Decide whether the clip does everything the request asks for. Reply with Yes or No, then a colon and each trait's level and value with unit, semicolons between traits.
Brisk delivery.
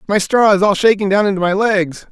Yes: fast, 255 wpm